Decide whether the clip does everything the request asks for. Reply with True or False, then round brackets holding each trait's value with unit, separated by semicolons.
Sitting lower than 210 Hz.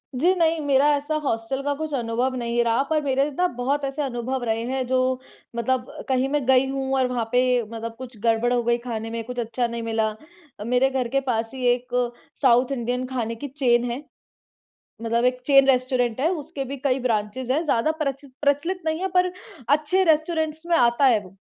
False (255 Hz)